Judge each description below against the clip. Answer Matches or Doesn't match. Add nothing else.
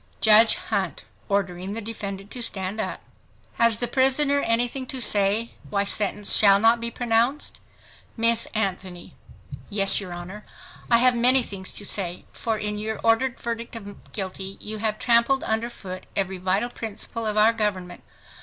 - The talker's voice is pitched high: Matches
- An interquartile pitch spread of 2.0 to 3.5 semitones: Matches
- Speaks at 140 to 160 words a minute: Matches